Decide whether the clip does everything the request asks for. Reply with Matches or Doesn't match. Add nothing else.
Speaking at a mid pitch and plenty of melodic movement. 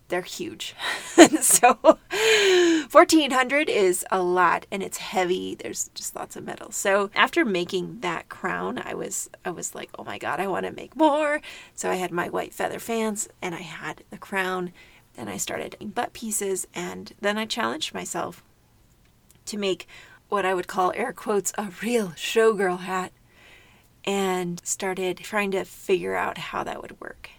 Doesn't match